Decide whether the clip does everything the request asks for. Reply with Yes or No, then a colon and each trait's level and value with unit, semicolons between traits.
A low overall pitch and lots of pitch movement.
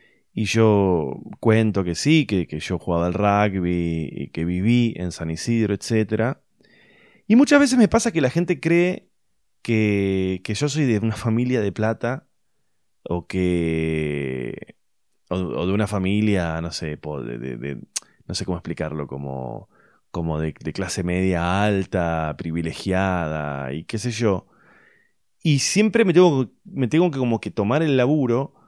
Yes: low, 105 Hz; wide, 6.8 semitones